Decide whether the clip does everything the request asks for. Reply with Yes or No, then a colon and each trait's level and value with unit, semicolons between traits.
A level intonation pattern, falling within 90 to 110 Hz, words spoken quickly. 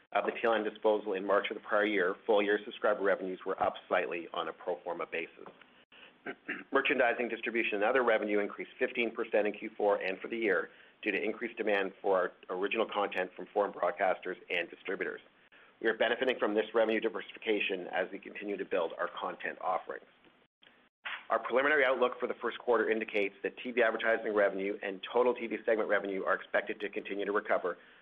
No: narrow, 2.3 semitones; low, 105 Hz; average, 185 wpm